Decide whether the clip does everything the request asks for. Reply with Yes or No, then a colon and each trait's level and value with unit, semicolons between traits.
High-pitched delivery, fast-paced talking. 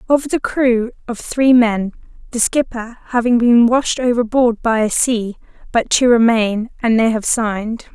No: high, 235 Hz; average, 165 wpm